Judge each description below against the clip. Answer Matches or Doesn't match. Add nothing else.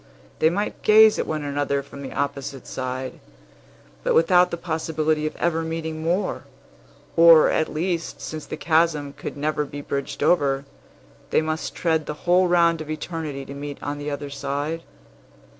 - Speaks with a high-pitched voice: Doesn't match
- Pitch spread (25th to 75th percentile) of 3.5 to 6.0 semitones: Doesn't match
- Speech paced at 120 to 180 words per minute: Matches